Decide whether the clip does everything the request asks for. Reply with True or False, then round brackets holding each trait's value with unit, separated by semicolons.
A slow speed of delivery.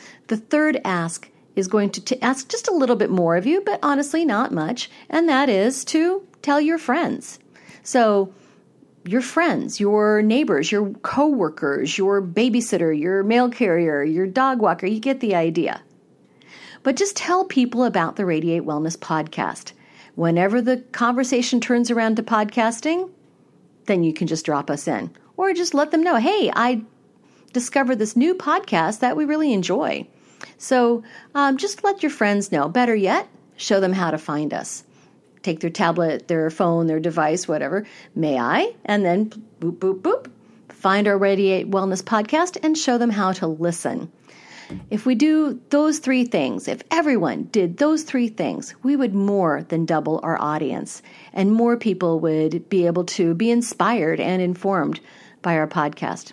False (165 wpm)